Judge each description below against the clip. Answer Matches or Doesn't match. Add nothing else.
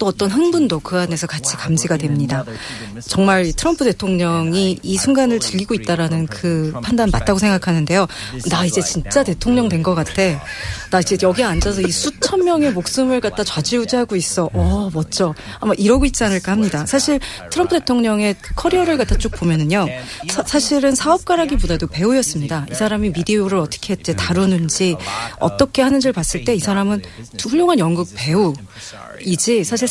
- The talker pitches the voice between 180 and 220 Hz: Matches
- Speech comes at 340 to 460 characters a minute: Matches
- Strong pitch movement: Matches